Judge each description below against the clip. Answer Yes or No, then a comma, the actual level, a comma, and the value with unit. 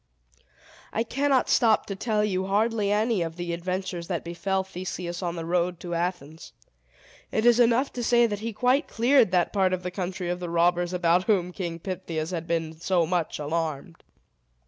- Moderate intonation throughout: Yes, average, 3.7 semitones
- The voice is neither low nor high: Yes, medium, 180 Hz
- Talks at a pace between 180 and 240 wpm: Yes, average, 185 wpm